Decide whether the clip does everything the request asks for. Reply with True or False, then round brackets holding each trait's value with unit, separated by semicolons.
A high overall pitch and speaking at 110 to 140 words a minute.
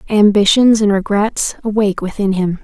True (205 Hz; 135 wpm)